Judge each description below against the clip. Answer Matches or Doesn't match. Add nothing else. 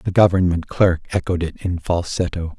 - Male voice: Matches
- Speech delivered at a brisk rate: Doesn't match